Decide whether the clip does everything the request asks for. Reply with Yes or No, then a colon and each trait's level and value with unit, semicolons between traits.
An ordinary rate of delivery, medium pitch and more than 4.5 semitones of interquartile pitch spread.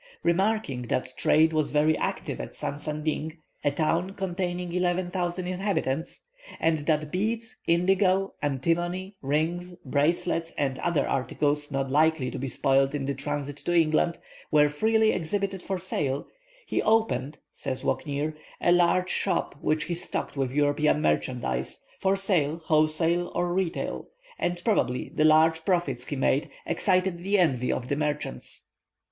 No: average, 145 wpm; medium, 160 Hz; average, 3.8 semitones